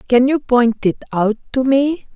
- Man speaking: No, female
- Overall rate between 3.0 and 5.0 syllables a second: Yes, 4.1 syllables/s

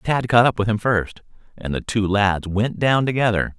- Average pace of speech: No, fast, 220 wpm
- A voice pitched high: No, low, 105 Hz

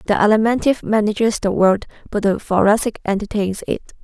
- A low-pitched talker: No, high, 210 Hz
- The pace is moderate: Yes, average, 150 wpm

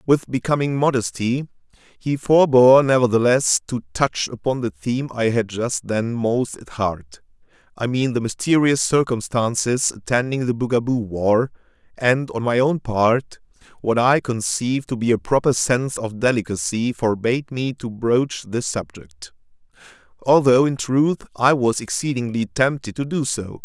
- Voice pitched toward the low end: Yes, low, 120 Hz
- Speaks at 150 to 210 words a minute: No, average, 140 wpm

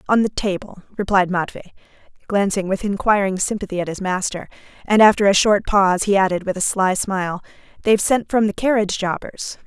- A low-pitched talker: No, high, 195 Hz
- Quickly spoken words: No, average, 180 wpm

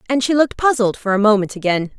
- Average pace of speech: No, fast, 240 wpm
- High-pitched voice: Yes, high, 225 Hz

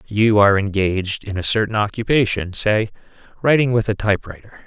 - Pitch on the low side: Yes, low, 105 Hz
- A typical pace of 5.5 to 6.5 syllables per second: Yes, 5.8 syllables/s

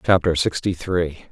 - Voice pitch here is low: Yes, very low, 85 Hz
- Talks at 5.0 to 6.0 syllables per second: No, 4.4 syllables/s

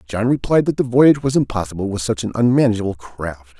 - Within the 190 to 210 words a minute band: Yes, average, 200 wpm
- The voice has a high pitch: No, low, 110 Hz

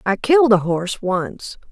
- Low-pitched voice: No, high, 215 Hz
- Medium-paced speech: Yes, average, 175 wpm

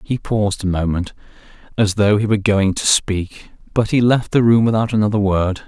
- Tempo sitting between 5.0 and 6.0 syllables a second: Yes, 5.3 syllables/s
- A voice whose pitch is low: Yes, low, 105 Hz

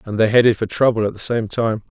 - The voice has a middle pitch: No, low, 110 Hz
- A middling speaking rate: No, fast, 275 wpm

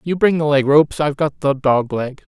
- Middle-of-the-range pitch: Yes, medium, 145 Hz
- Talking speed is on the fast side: Yes, fast, 230 wpm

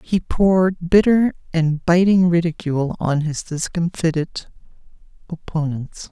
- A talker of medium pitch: Yes, medium, 170 Hz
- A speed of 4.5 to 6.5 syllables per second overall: No, 4.3 syllables/s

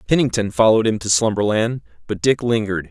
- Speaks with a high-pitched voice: No, low, 110 Hz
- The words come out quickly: No, average, 165 wpm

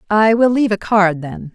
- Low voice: No, high, 205 Hz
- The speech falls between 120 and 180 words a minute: No, fast, 235 wpm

